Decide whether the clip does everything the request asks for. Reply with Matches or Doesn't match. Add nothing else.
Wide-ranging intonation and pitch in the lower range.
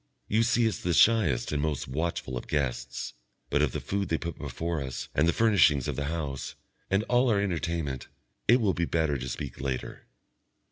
Matches